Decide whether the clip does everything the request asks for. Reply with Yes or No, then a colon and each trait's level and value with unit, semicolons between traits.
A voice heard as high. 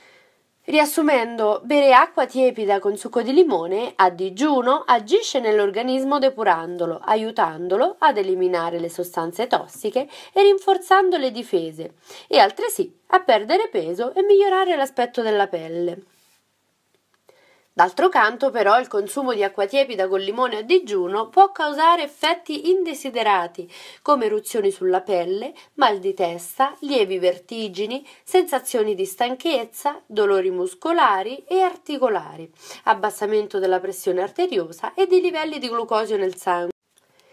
Yes: very high, 250 Hz